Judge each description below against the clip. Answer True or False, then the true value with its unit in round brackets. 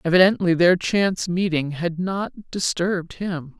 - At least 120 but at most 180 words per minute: True (135 wpm)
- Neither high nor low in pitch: True (175 Hz)